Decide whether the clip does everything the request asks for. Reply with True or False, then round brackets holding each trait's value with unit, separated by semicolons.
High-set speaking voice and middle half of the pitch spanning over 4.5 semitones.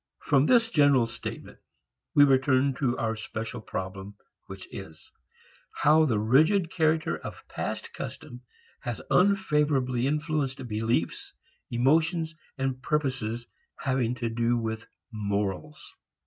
False (130 Hz; 5.0 semitones)